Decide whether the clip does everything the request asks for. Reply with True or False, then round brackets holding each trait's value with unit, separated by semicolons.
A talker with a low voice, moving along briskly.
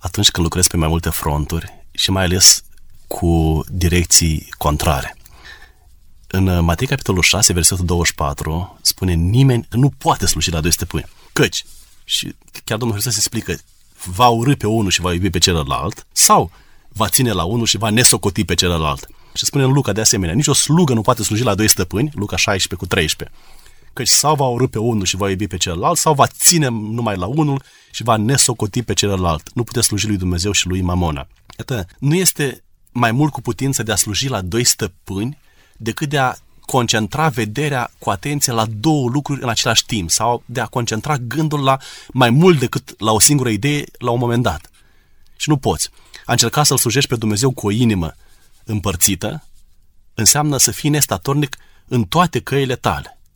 True (110 Hz; 185 wpm)